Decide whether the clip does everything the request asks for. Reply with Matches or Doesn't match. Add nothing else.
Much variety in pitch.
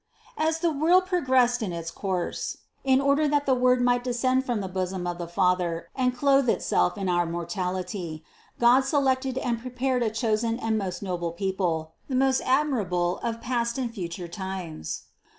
Matches